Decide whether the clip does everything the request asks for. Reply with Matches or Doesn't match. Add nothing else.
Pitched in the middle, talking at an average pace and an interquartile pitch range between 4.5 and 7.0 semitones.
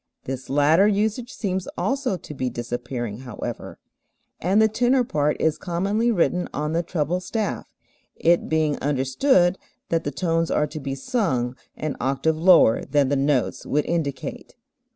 Matches